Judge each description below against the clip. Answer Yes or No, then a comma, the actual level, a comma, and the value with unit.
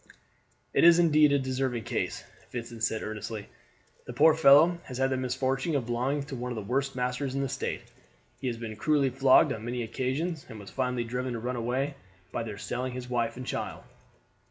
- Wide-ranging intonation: No, narrow, 2.6 semitones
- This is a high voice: No, low, 125 Hz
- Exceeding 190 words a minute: Yes, average, 200 wpm